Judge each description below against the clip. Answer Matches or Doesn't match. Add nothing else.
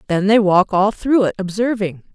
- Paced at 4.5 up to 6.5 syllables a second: Matches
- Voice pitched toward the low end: Doesn't match